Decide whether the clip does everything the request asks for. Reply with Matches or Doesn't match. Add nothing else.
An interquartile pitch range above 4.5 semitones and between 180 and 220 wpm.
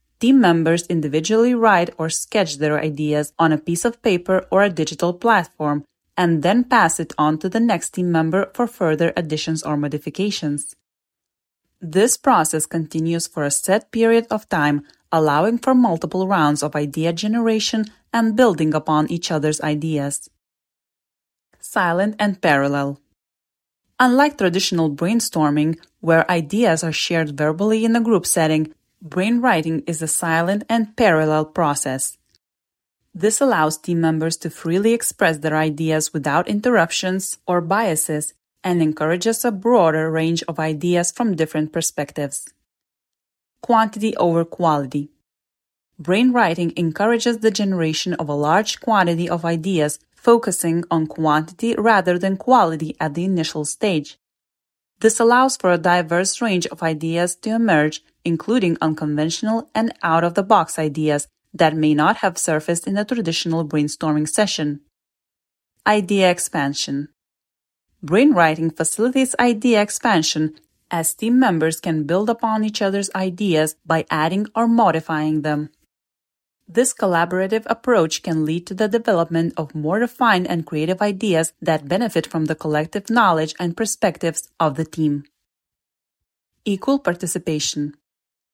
Doesn't match